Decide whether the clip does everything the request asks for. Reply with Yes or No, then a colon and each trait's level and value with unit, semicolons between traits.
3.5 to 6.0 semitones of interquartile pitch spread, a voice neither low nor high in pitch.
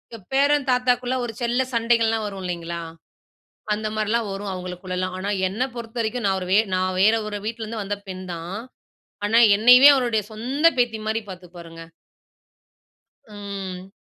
No: average, 4.0 semitones; high, 215 Hz